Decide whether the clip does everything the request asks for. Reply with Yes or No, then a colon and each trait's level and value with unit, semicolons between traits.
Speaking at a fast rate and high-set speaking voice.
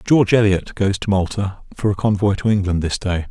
No: fast, 220 wpm; low, 100 Hz